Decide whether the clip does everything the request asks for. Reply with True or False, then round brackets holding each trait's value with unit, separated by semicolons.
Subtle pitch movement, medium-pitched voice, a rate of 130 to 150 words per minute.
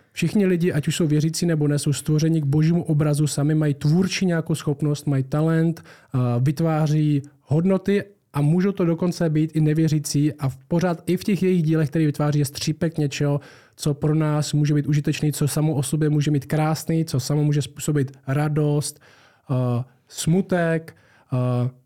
False (2.0 semitones; 150 Hz; 160 wpm)